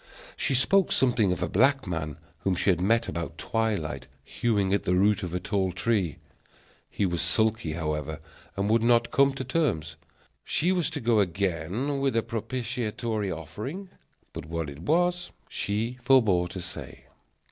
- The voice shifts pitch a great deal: Yes, wide, 6.1 semitones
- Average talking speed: Yes, average, 165 wpm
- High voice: No, low, 105 Hz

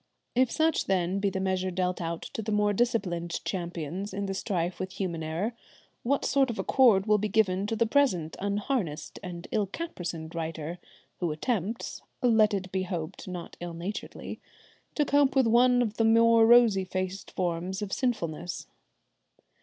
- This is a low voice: No, high, 195 Hz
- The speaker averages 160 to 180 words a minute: Yes, average, 170 wpm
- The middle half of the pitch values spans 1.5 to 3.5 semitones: No, average, 4.5 semitones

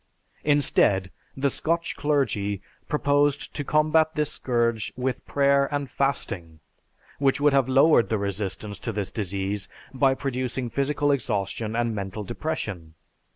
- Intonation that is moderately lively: No, wide, 5.8 semitones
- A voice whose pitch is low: Yes, low, 130 Hz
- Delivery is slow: Yes, slow, 130 wpm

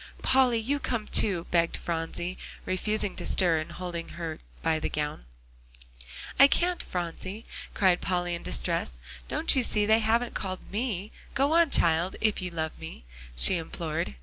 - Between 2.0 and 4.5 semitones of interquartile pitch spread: No, average, 5.1 semitones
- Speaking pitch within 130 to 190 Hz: Yes, medium, 185 Hz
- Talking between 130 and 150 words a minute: No, average, 160 wpm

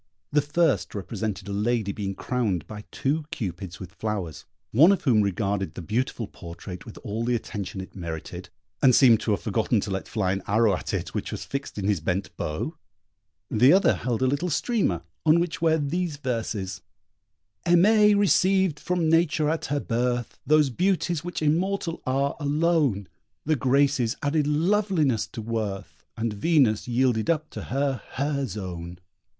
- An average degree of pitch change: No, wide, 7.2 semitones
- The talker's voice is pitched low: Yes, low, 125 Hz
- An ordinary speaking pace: Yes, average, 165 wpm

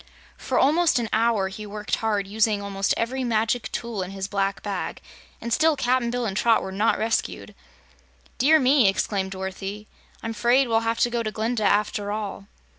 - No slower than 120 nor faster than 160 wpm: No, average, 185 wpm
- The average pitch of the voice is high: Yes, high, 220 Hz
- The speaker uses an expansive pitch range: No, average, 2.9 semitones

